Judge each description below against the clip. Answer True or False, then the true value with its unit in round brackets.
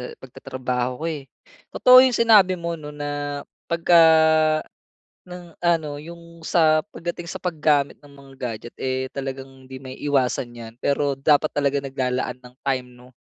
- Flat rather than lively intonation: False (4.2 semitones)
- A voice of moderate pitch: True (145 Hz)